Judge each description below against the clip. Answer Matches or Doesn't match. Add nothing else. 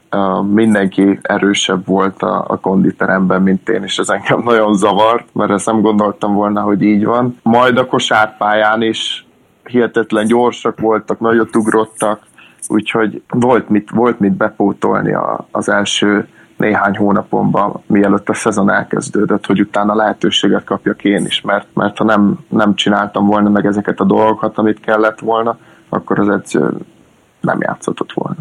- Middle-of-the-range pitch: Doesn't match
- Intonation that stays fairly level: Matches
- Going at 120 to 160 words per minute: Matches